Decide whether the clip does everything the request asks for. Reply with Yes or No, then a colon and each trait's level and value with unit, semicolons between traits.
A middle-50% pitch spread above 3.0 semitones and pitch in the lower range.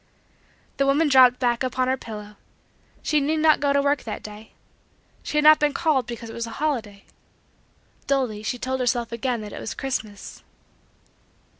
No: average, 3.9 semitones; very high, 255 Hz